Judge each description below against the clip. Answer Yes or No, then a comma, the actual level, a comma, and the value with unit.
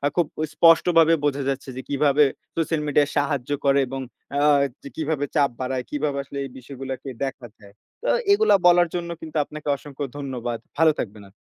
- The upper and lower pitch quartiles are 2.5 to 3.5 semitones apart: Yes, average, 2.9 semitones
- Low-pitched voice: No, medium, 145 Hz